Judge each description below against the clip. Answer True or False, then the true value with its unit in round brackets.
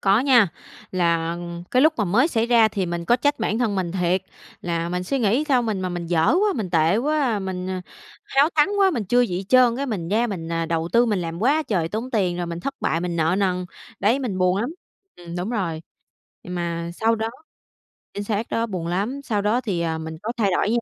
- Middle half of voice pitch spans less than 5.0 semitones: False (5.5 semitones)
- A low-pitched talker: False (200 Hz)